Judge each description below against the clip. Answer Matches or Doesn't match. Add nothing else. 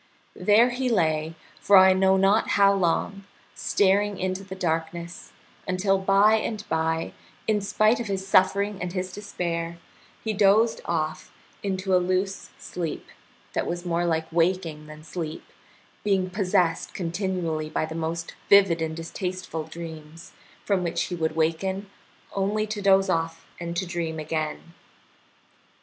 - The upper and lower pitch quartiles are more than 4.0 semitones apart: Doesn't match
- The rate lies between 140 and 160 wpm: Matches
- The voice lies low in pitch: Doesn't match